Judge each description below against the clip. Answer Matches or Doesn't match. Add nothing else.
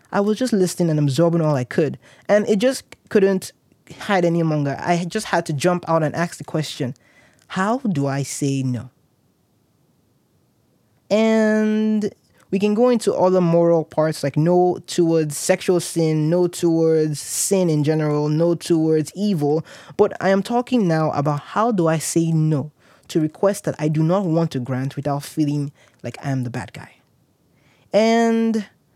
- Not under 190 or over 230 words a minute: Doesn't match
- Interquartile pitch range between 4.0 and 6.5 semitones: Matches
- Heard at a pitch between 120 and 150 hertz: Doesn't match